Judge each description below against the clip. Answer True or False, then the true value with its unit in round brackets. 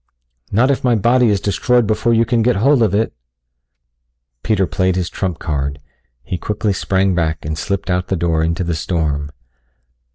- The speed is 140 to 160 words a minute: False (175 wpm)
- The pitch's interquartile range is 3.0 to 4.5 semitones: False (5.1 semitones)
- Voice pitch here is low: True (95 Hz)